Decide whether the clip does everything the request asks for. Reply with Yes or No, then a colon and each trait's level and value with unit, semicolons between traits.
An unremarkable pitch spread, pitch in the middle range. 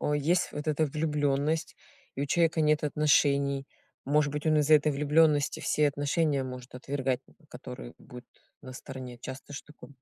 No: narrow, 1.9 semitones; medium, 145 Hz